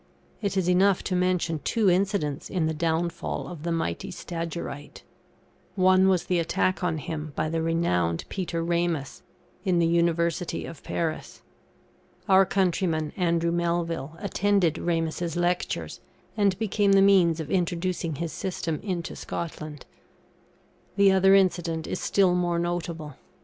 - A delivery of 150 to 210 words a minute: No, average, 140 wpm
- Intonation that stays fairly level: Yes, narrow, 2.2 semitones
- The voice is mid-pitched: Yes, medium, 170 Hz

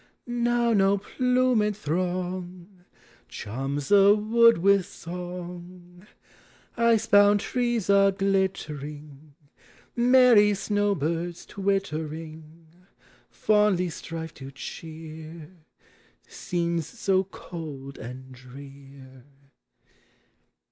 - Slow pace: Yes, slow, 80 wpm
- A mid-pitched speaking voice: Yes, medium, 180 Hz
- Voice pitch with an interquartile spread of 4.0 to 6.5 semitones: Yes, average, 4.8 semitones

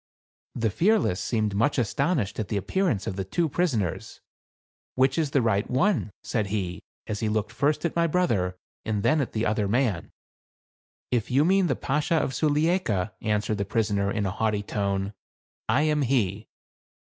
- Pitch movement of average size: No, wide, 6.6 semitones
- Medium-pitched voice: No, low, 110 Hz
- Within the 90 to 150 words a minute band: No, average, 185 wpm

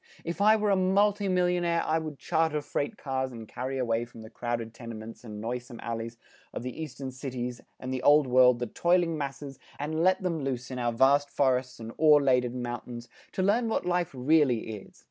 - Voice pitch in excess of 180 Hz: No, low, 135 Hz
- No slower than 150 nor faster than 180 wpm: No, average, 200 wpm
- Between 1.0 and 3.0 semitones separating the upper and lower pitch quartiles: No, average, 5.2 semitones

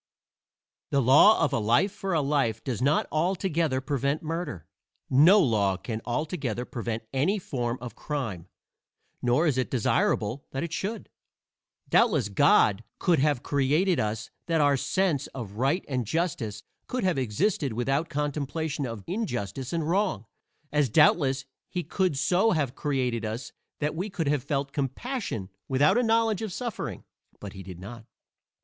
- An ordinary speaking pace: Yes, average, 160 wpm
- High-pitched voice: No, medium, 140 Hz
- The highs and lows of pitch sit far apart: Yes, wide, 5.9 semitones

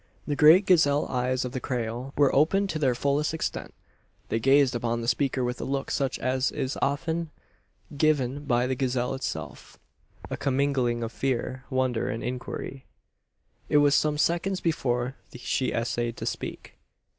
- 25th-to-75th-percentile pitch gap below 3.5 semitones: Yes, average, 2.7 semitones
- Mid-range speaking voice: No, low, 130 Hz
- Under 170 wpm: Yes, average, 160 wpm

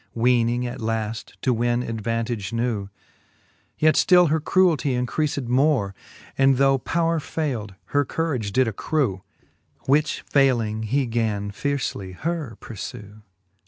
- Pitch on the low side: Yes, low, 125 Hz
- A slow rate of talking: Yes, slow, 125 wpm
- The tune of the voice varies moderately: Yes, average, 4.3 semitones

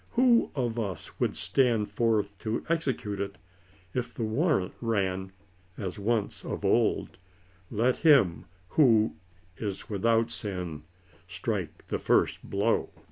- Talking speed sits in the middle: No, slow, 130 wpm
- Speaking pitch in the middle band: No, low, 110 Hz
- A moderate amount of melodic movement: Yes, average, 3.7 semitones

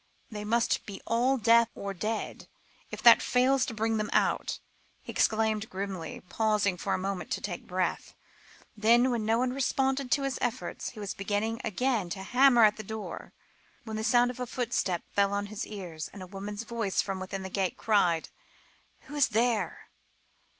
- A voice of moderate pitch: No, high, 215 Hz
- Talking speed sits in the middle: Yes, average, 185 wpm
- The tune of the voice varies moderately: Yes, average, 3.3 semitones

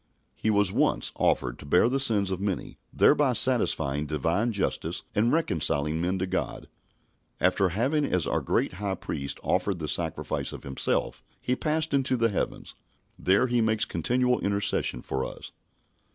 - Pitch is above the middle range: No, low, 100 Hz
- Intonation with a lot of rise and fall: Yes, wide, 6.2 semitones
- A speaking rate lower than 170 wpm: Yes, average, 160 wpm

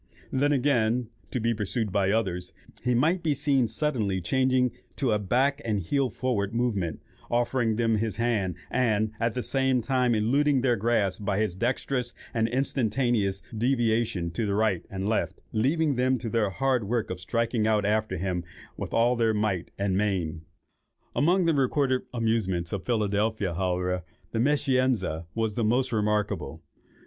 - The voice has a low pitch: Yes, low, 115 Hz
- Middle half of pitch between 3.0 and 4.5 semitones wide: Yes, average, 4.0 semitones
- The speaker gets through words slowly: No, average, 160 wpm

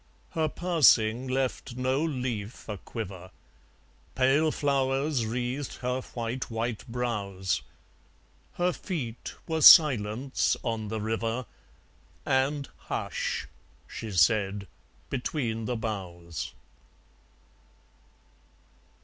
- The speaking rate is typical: No, slow, 90 wpm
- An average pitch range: Yes, average, 3.6 semitones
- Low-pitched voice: Yes, low, 120 Hz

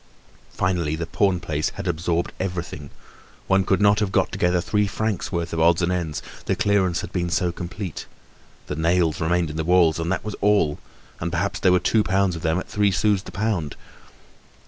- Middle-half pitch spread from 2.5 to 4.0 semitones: Yes, average, 2.9 semitones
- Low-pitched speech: Yes, very low, 90 Hz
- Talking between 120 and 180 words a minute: No, average, 200 wpm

